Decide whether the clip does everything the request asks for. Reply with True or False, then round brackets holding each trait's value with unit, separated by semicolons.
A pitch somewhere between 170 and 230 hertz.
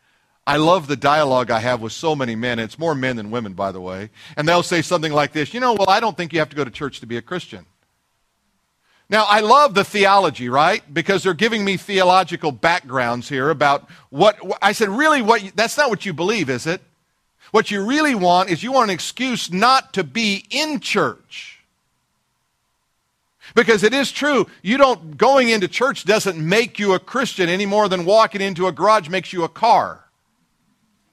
True (185 Hz)